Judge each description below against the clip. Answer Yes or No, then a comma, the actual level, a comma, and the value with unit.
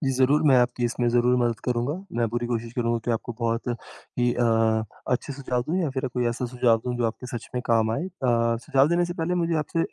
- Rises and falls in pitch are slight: Yes, narrow, 2.3 semitones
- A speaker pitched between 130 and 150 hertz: No, low, 120 Hz